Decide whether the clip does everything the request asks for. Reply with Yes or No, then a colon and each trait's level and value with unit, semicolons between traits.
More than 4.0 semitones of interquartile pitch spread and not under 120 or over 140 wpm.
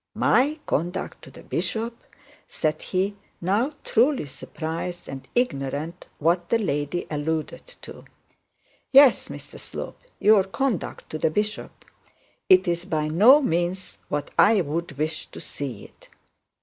Yes: wide, 5.6 semitones; slow, 135 wpm